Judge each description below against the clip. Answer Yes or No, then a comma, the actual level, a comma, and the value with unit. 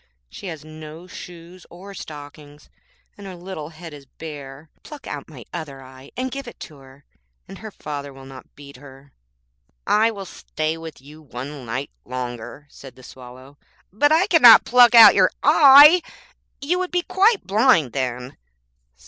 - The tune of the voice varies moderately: No, wide, 7.5 semitones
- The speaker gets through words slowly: No, average, 165 wpm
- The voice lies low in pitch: No, medium, 155 Hz